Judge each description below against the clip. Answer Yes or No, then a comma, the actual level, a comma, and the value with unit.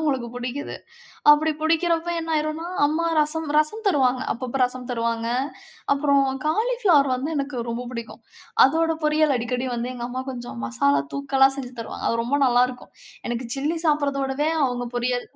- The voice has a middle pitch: No, very high, 270 Hz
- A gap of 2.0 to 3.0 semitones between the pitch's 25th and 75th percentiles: No, average, 3.8 semitones